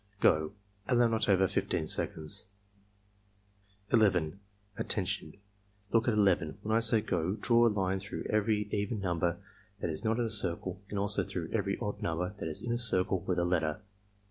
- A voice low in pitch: Yes, low, 100 Hz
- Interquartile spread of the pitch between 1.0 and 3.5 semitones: No, average, 3.9 semitones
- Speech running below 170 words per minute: No, average, 180 wpm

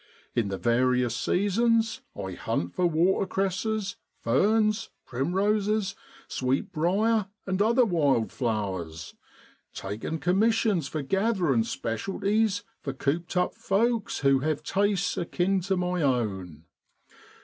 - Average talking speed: No, slow, 105 wpm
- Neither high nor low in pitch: Yes, medium, 180 Hz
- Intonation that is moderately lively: No, wide, 8.2 semitones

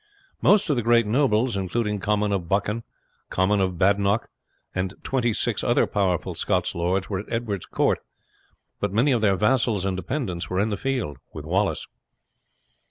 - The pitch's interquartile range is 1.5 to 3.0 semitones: No, average, 3.8 semitones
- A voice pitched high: No, low, 100 Hz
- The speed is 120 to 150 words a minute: No, average, 165 wpm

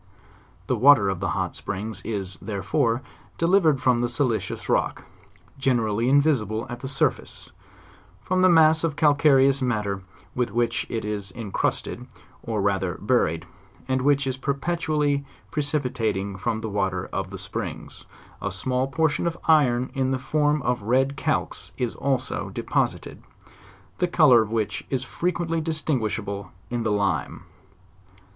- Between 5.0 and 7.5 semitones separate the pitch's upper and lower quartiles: Yes, wide, 5.4 semitones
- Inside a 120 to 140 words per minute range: No, average, 150 wpm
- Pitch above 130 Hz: No, low, 125 Hz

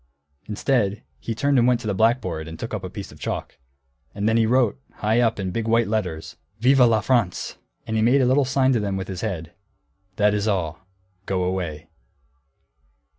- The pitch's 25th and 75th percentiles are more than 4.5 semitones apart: No, average, 4.2 semitones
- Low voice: Yes, low, 110 Hz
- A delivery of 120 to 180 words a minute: No, average, 200 wpm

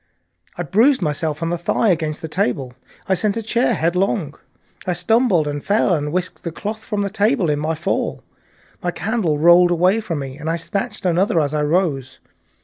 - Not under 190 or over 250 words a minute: Yes, average, 195 wpm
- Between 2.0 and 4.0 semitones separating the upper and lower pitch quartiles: No, average, 4.7 semitones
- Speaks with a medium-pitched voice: Yes, medium, 175 Hz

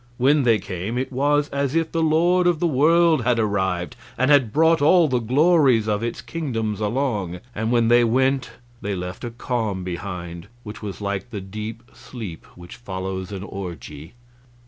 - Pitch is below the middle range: Yes, low, 115 Hz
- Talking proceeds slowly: No, average, 175 wpm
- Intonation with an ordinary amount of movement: No, wide, 6.2 semitones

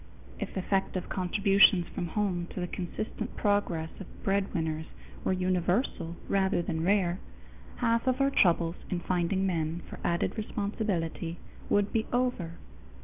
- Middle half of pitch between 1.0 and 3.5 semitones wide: Yes, average, 3.0 semitones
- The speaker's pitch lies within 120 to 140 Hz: No, medium, 185 Hz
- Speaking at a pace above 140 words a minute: No, slow, 135 wpm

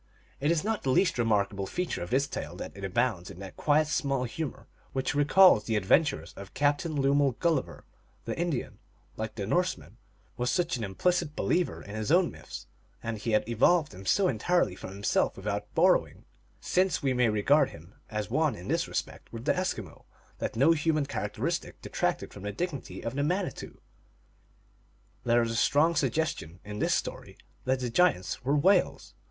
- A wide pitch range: Yes, wide, 7.1 semitones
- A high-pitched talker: No, low, 130 Hz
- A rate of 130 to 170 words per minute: No, average, 180 wpm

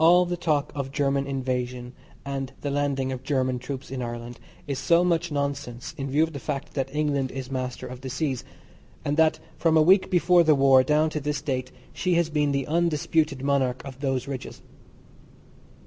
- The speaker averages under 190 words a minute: No, average, 195 wpm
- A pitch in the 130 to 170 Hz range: Yes, medium, 140 Hz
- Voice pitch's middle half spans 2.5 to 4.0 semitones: Yes, average, 2.8 semitones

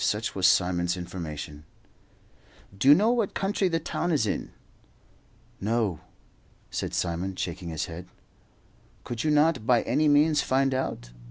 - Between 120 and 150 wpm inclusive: Yes, average, 145 wpm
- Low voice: Yes, low, 110 Hz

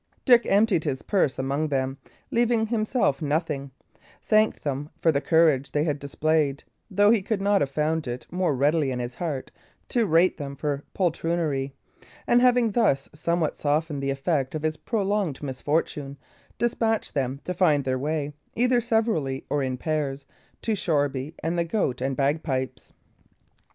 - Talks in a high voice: No, medium, 155 Hz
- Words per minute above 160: No, average, 155 wpm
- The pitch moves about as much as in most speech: No, wide, 5.8 semitones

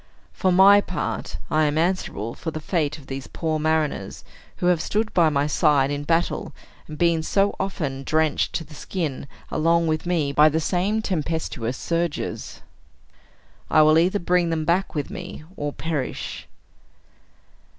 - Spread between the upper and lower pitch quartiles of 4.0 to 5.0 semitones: No, average, 3.0 semitones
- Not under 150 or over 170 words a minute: Yes, average, 160 wpm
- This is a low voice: No, medium, 160 Hz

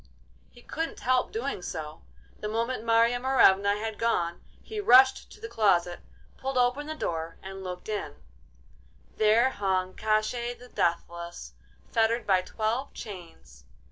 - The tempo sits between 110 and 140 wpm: Yes, slow, 135 wpm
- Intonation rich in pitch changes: Yes, wide, 6.0 semitones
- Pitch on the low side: No, high, 215 Hz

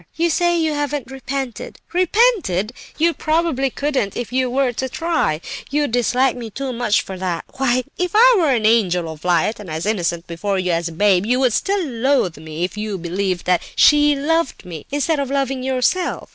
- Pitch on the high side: Yes, very high, 250 Hz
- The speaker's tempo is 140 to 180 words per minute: No, average, 195 wpm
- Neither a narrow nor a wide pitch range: No, wide, 7.6 semitones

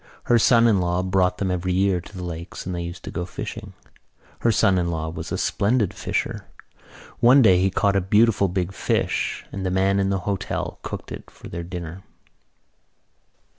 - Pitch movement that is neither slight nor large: No, narrow, 1.9 semitones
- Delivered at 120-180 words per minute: No, average, 195 wpm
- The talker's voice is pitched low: Yes, very low, 95 Hz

